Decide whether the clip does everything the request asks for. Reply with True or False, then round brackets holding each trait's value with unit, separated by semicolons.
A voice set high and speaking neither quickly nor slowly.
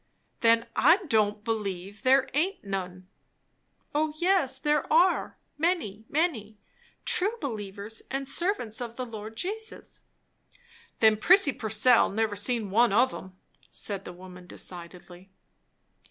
False (225 Hz; 125 wpm)